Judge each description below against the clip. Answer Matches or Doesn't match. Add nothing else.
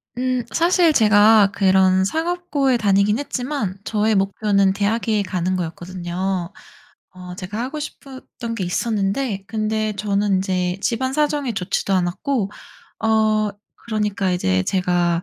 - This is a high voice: Matches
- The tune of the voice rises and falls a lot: Doesn't match